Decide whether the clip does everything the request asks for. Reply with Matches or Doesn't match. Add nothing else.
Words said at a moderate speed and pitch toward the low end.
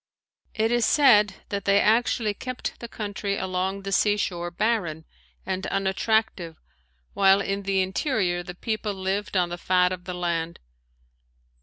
Doesn't match